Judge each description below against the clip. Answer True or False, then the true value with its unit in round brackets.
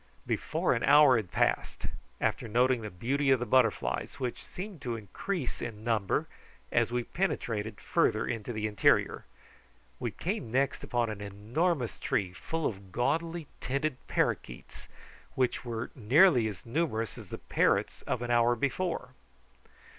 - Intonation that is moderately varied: True (4.1 semitones)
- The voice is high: False (120 Hz)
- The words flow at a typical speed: True (145 wpm)